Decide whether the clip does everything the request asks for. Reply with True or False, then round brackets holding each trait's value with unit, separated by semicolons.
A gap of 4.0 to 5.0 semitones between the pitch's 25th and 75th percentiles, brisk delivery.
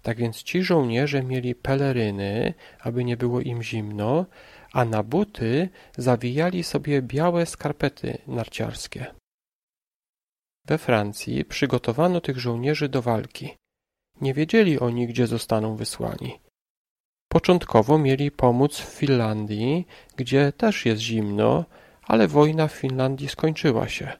False (4.5 semitones; 115 wpm)